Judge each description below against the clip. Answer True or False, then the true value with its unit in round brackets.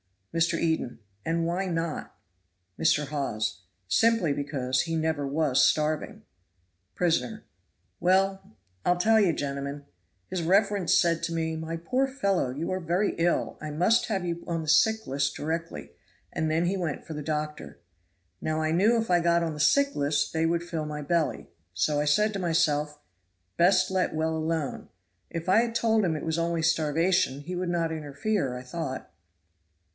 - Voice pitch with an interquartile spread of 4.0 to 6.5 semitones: False (3.2 semitones)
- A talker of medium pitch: True (165 Hz)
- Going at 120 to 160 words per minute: False (170 wpm)